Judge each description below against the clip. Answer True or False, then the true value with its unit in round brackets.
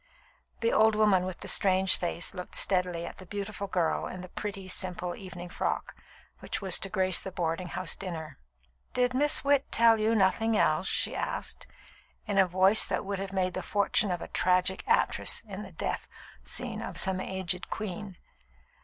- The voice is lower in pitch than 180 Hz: False (190 Hz)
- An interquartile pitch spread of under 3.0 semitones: True (2.4 semitones)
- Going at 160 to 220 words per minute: True (180 wpm)